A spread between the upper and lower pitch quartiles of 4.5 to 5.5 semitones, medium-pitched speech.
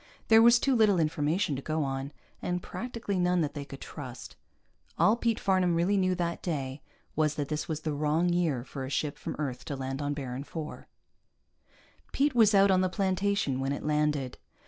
Yes: average, 5.0 semitones; medium, 155 Hz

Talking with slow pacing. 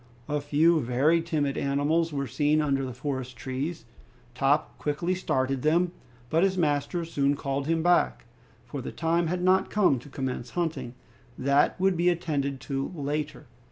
No: average, 160 wpm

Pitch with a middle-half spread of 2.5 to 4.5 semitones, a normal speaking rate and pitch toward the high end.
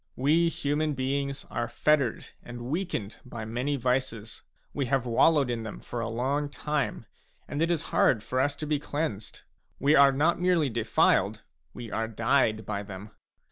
No: average, 4.2 semitones; average, 170 wpm; low, 135 Hz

